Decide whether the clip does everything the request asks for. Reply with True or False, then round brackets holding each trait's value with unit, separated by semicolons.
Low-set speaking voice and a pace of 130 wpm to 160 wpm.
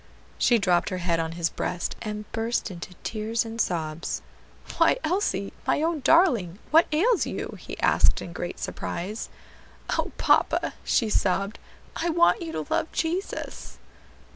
False (215 Hz; 150 wpm)